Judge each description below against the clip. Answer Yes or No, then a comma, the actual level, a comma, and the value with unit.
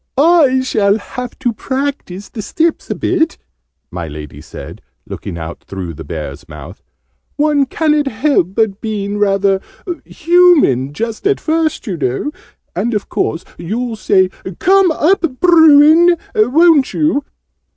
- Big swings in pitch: Yes, wide, 8.4 semitones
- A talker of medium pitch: No, very high, 250 Hz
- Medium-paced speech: No, slow, 130 wpm